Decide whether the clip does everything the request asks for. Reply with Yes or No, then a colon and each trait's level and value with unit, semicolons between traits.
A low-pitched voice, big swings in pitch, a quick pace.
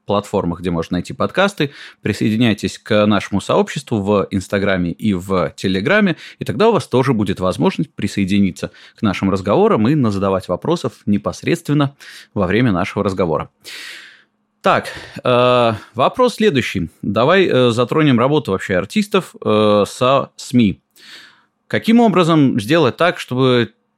No: low, 115 Hz; wide, 8.0 semitones; average, 125 wpm